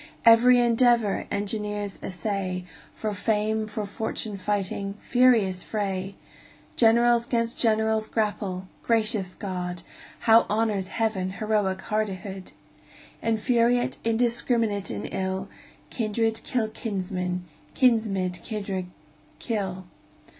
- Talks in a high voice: Yes, high, 210 Hz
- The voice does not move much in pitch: No, average, 3.0 semitones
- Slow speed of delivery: Yes, slow, 95 wpm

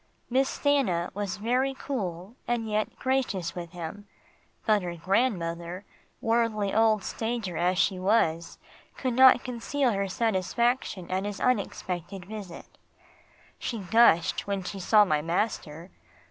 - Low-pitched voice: No, high, 205 Hz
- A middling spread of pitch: Yes, average, 4.7 semitones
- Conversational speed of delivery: No, slow, 130 wpm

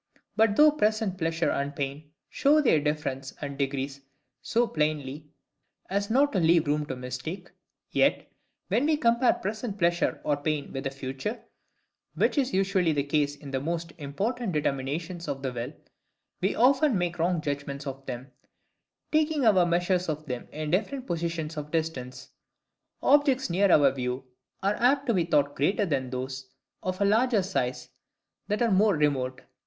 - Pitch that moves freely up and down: Yes, wide, 6.8 semitones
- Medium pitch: Yes, medium, 165 Hz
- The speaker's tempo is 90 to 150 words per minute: No, average, 160 wpm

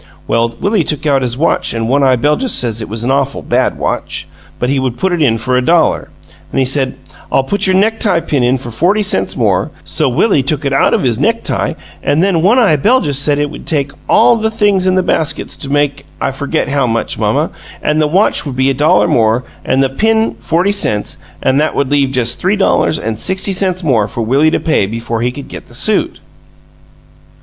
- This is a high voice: No, medium, 145 Hz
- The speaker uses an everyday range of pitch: No, wide, 6.3 semitones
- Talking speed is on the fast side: Yes, fast, 225 wpm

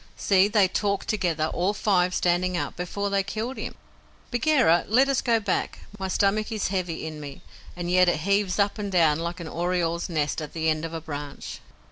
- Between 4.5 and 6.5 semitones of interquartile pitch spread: No, average, 3.6 semitones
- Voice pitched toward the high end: No, medium, 180 Hz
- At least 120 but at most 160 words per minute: No, average, 200 wpm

